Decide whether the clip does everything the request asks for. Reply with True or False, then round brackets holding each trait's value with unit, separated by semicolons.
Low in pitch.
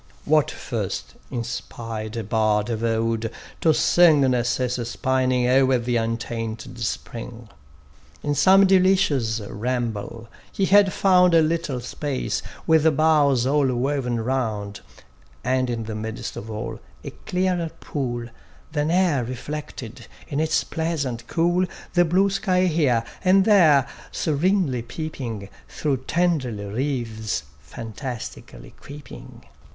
True (130 Hz)